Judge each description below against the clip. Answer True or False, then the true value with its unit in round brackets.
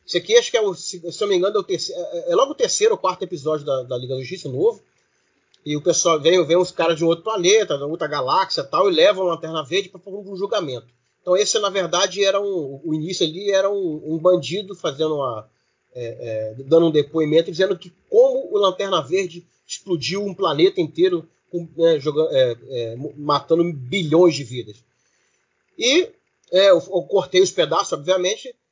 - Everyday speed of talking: False (205 wpm)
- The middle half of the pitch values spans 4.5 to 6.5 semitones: True (4.8 semitones)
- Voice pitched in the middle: True (180 Hz)